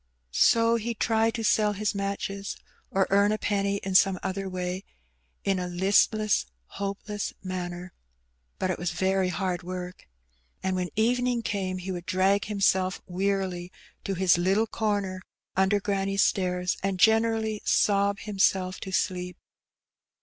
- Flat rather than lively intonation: Yes, narrow, 2.0 semitones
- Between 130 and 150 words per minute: Yes, average, 145 wpm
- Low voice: No, high, 195 Hz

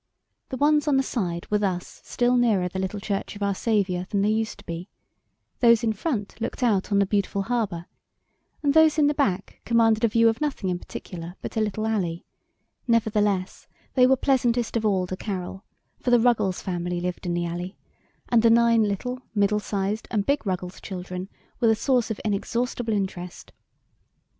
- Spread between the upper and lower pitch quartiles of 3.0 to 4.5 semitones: Yes, average, 3.9 semitones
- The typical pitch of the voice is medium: No, high, 210 Hz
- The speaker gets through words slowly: No, average, 190 wpm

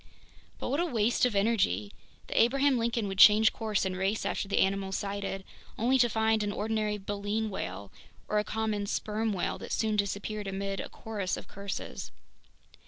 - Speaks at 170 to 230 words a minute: Yes, average, 175 wpm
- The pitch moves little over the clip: Yes, narrow, 2.0 semitones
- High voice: Yes, high, 210 Hz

